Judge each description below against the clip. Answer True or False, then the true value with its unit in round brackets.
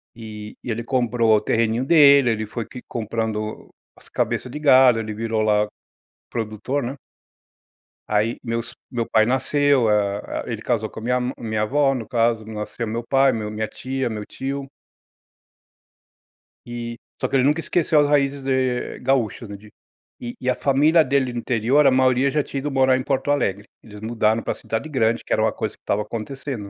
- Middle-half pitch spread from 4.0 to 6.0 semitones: False (3.5 semitones)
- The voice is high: False (120 Hz)